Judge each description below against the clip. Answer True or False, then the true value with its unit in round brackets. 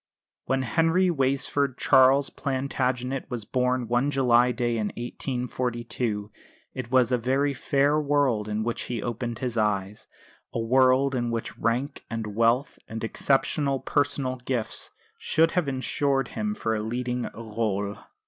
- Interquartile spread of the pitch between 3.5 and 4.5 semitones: False (2.9 semitones)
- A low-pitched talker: True (125 Hz)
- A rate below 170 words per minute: True (140 wpm)